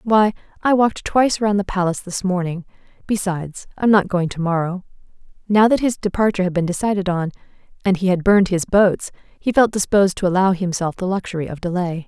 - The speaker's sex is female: Yes, female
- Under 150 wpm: No, average, 195 wpm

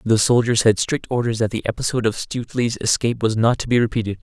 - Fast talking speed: Yes, fast, 225 wpm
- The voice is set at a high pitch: No, low, 115 Hz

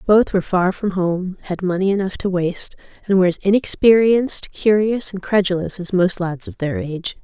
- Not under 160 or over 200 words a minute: Yes, average, 190 wpm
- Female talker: Yes, female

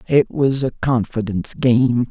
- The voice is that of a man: Yes, male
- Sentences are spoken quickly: No, average, 140 wpm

